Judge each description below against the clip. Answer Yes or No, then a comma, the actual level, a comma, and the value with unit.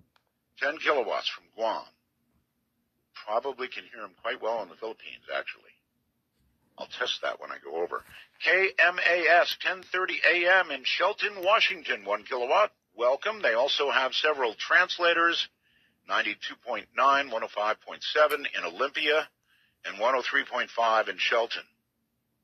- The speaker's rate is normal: No, slow, 110 wpm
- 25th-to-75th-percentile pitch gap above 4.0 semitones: Yes, average, 5.1 semitones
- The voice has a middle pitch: Yes, medium, 150 Hz